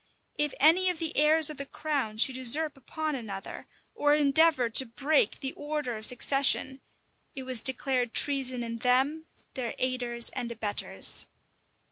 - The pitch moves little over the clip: No, average, 3.6 semitones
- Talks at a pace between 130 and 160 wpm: Yes, average, 150 wpm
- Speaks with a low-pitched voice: No, very high, 265 Hz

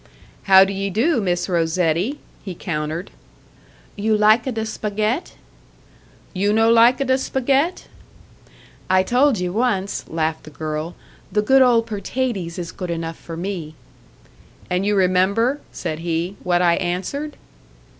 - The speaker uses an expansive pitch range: No, average, 4.7 semitones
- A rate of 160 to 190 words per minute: No, slow, 135 wpm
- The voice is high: Yes, high, 195 Hz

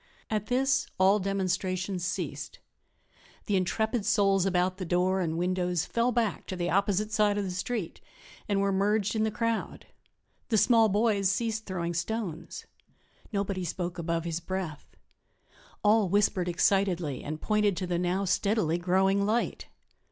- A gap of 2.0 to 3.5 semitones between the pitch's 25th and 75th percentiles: Yes, average, 2.9 semitones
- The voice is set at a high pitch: Yes, high, 195 Hz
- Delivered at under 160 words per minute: Yes, average, 150 wpm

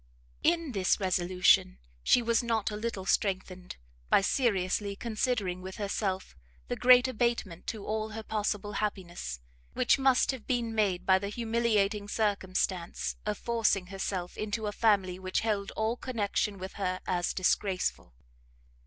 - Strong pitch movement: No, average, 3.2 semitones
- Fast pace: No, average, 145 wpm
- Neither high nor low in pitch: No, high, 205 Hz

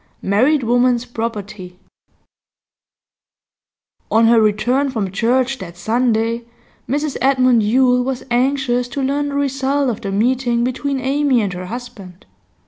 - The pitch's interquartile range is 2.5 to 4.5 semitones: Yes, average, 3.2 semitones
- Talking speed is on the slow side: Yes, slow, 130 wpm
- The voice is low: No, high, 245 Hz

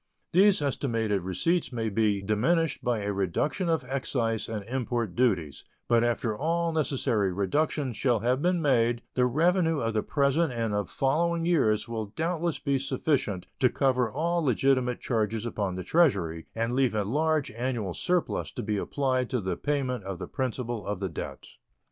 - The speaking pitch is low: Yes, low, 125 Hz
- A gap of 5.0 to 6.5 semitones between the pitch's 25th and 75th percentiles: Yes, wide, 5.5 semitones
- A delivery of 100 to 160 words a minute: No, average, 170 wpm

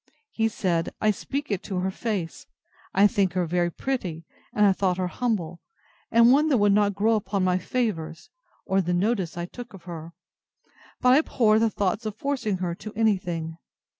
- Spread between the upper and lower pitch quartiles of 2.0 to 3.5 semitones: No, average, 4.0 semitones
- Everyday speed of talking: Yes, average, 195 wpm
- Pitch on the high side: Yes, high, 195 Hz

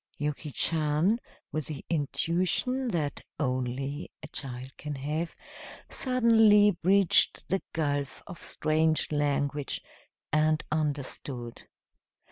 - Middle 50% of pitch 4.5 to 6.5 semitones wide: No, average, 3.3 semitones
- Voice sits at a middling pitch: Yes, medium, 155 Hz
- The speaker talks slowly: Yes, slow, 95 wpm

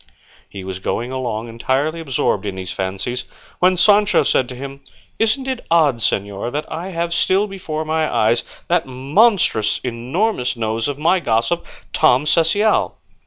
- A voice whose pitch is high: No, low, 135 Hz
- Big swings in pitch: Yes, wide, 6.8 semitones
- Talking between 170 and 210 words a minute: No, average, 155 wpm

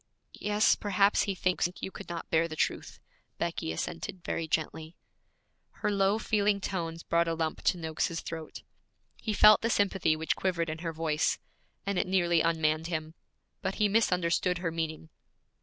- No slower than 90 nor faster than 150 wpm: No, average, 165 wpm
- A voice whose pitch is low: No, medium, 170 Hz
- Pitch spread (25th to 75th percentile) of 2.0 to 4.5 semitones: Yes, average, 3.3 semitones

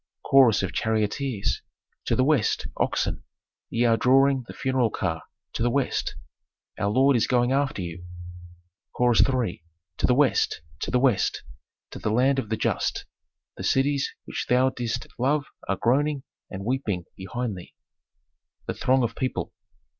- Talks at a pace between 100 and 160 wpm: Yes, average, 155 wpm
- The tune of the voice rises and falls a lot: No, average, 3.6 semitones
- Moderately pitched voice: No, low, 125 Hz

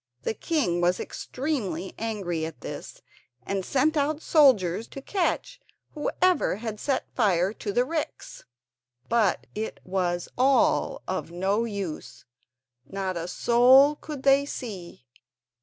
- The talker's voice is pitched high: Yes, high, 215 Hz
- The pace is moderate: No, slow, 125 wpm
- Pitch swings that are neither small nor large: No, wide, 7.4 semitones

